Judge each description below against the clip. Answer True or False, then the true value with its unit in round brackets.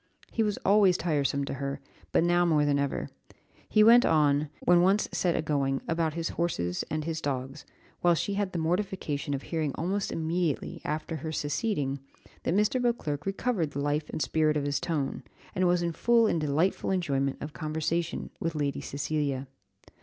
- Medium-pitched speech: True (160 Hz)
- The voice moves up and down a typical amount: True (3.7 semitones)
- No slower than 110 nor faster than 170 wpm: False (180 wpm)